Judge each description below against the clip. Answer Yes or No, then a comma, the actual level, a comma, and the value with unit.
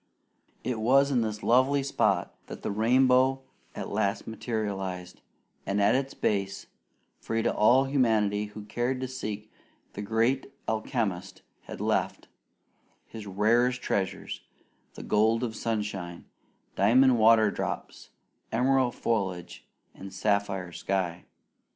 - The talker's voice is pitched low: Yes, low, 110 Hz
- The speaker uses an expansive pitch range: No, average, 3.9 semitones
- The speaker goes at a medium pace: No, slow, 120 wpm